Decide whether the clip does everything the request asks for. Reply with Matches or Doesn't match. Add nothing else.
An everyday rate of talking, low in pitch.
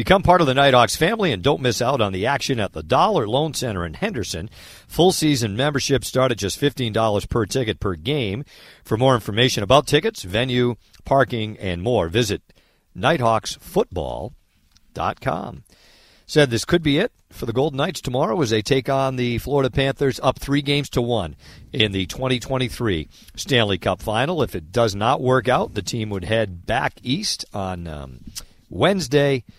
Matches